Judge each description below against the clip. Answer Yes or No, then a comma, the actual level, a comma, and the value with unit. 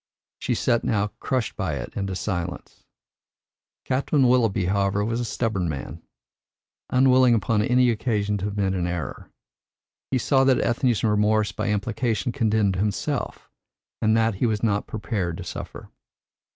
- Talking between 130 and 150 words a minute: Yes, average, 145 wpm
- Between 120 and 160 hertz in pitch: No, low, 105 Hz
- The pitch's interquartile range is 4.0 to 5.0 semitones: No, average, 3.4 semitones